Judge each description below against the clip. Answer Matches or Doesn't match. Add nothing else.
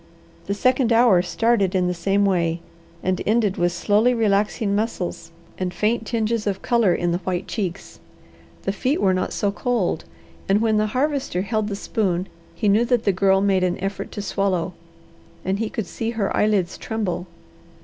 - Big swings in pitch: Doesn't match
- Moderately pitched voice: Doesn't match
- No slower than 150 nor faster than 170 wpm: Doesn't match